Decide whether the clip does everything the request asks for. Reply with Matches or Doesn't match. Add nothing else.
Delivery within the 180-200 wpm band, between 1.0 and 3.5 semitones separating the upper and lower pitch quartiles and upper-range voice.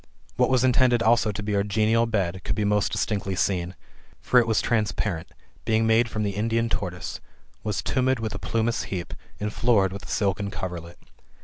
Doesn't match